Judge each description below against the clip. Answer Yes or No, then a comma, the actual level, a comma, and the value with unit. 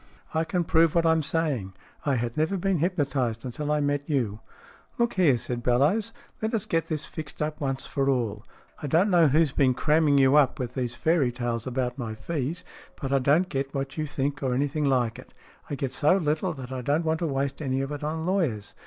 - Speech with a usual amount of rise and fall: Yes, average, 3.7 semitones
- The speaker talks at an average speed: No, fast, 225 wpm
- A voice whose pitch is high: No, medium, 145 Hz